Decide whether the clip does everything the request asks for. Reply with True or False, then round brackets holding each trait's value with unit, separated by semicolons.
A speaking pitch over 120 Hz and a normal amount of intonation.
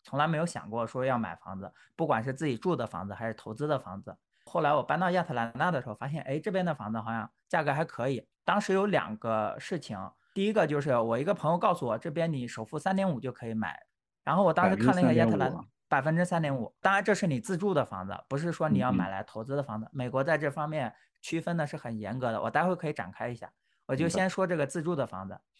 False (140 Hz; 7.1 semitones)